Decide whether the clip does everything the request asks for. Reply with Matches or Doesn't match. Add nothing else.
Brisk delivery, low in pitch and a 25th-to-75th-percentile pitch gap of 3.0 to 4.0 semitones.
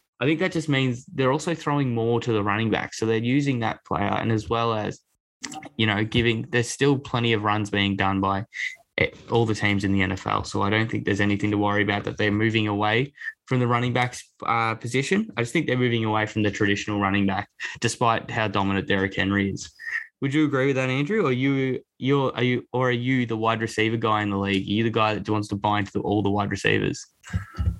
Matches